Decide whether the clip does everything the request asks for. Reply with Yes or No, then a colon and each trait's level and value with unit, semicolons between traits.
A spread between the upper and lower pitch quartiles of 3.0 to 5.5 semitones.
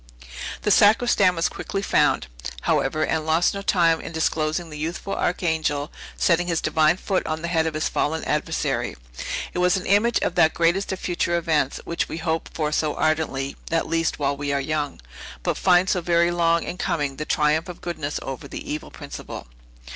No: narrow, 2.4 semitones